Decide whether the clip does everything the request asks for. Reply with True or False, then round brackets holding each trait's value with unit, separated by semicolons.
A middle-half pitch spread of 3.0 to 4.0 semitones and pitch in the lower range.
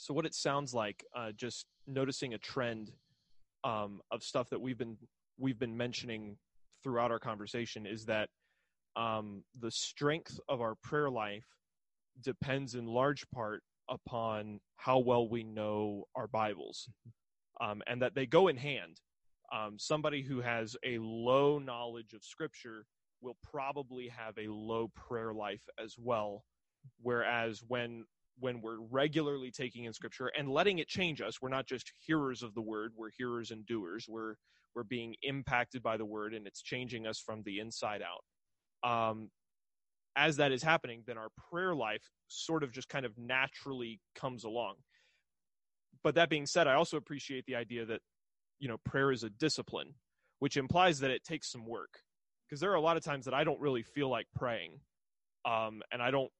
True (3.4 semitones; 120 Hz)